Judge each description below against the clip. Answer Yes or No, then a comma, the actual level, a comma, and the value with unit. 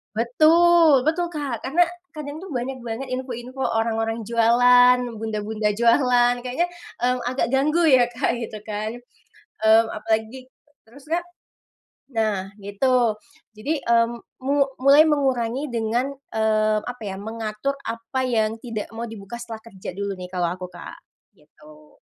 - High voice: Yes, high, 235 Hz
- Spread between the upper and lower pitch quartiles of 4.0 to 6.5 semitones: No, average, 3.4 semitones